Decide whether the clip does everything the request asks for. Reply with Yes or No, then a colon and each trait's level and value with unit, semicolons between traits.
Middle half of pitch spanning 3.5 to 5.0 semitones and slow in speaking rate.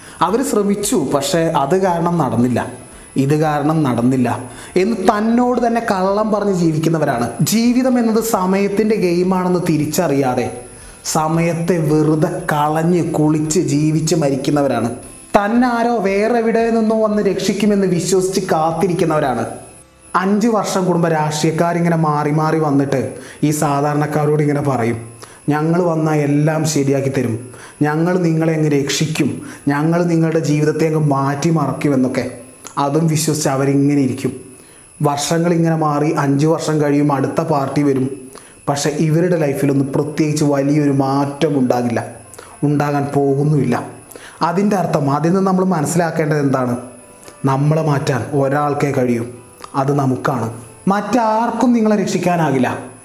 No: average, 4.1 semitones; average, 110 wpm